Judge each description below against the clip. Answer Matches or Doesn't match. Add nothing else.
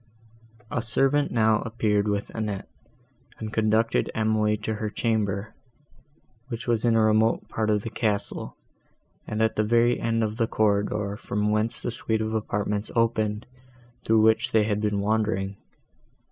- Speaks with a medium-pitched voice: Doesn't match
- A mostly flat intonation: Matches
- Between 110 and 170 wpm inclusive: Matches